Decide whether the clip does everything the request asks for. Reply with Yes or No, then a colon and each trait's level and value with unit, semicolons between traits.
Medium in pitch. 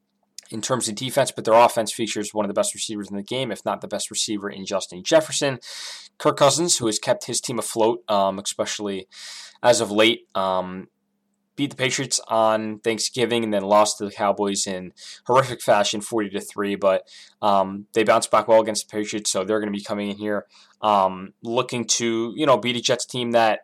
No: low, 110 Hz